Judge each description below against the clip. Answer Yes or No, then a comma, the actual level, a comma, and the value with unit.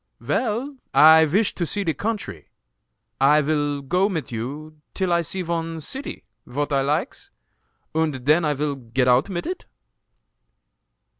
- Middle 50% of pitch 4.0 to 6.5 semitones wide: Yes, average, 4.4 semitones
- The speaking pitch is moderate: Yes, medium, 155 Hz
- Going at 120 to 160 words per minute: Yes, average, 150 wpm